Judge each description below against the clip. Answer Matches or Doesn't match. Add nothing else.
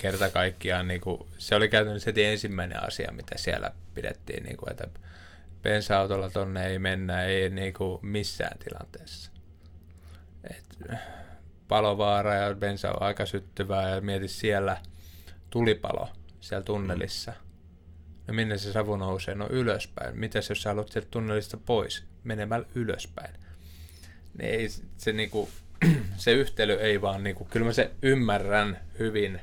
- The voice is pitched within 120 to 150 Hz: Doesn't match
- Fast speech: Doesn't match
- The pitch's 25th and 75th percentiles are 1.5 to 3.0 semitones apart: Doesn't match